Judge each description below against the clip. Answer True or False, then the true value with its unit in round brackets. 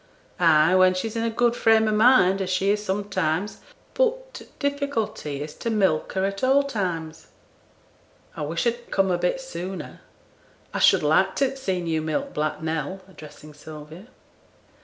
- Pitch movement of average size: False (6.1 semitones)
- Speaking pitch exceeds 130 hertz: True (190 Hz)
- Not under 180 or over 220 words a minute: False (170 wpm)